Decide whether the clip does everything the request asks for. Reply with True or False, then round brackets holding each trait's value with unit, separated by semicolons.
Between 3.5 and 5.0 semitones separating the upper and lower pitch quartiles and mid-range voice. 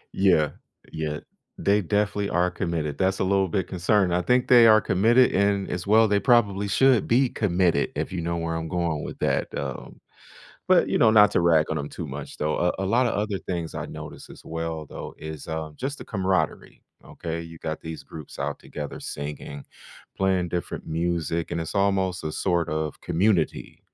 False (3.9 semitones; 90 Hz)